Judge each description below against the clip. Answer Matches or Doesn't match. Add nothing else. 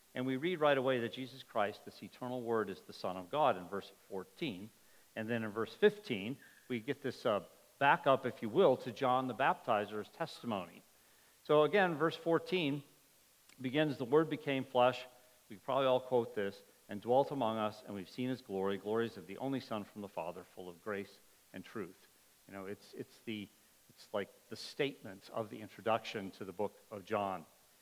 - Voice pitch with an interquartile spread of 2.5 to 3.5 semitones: Doesn't match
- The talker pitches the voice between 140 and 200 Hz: Doesn't match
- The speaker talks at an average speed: Matches